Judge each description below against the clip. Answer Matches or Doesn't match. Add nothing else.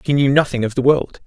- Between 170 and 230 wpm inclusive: Doesn't match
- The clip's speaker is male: Matches